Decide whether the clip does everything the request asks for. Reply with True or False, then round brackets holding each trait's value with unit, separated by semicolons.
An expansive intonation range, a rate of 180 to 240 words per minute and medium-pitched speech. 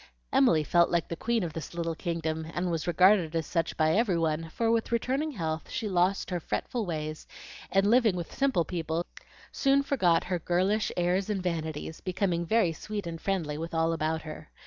False (3.5 semitones; 190 wpm; 175 Hz)